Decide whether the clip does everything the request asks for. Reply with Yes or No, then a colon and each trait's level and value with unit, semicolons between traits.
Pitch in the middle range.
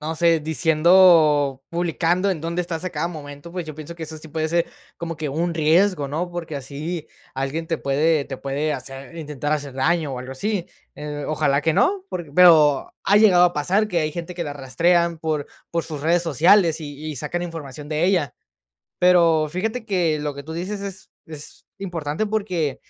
Yes: medium, 160 Hz